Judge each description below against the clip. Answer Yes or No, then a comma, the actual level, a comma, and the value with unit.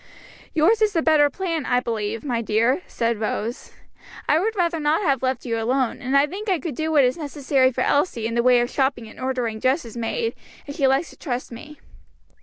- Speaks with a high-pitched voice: Yes, very high, 265 Hz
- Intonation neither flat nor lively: Yes, average, 4.9 semitones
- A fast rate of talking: Yes, fast, 215 wpm